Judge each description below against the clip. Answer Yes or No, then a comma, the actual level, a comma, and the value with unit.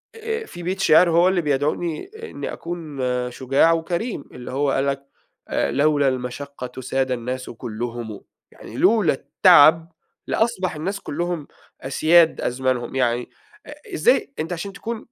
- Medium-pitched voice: Yes, medium, 150 Hz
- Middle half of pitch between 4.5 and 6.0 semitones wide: Yes, average, 5.3 semitones